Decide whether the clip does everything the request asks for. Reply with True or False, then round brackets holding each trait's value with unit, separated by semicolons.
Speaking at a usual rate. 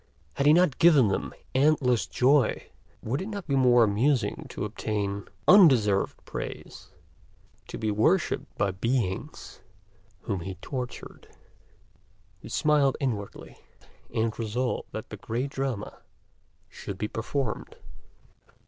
False (120 wpm)